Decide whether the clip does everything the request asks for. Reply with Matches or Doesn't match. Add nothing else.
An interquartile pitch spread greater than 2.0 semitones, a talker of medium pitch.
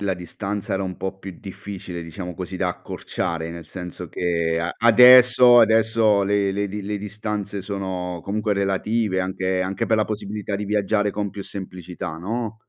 Doesn't match